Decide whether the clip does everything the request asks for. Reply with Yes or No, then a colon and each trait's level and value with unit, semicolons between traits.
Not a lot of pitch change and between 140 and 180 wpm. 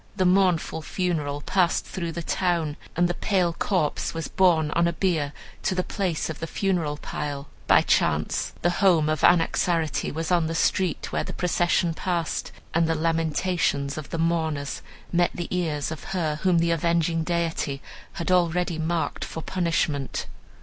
Yes: narrow, 2.1 semitones; average, 165 wpm